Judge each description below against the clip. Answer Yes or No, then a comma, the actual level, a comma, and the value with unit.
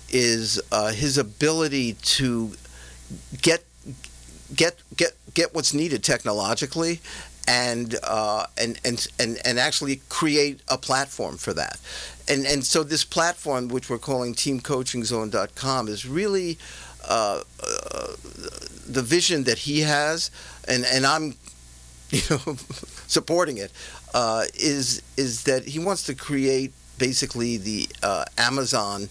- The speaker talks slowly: Yes, slow, 125 wpm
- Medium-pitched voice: No, low, 130 Hz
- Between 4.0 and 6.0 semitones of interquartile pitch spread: Yes, average, 4.4 semitones